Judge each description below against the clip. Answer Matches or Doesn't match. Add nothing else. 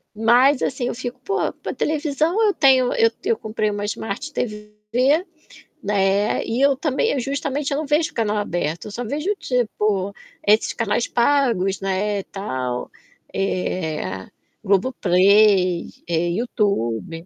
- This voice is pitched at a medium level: Doesn't match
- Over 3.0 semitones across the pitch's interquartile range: Matches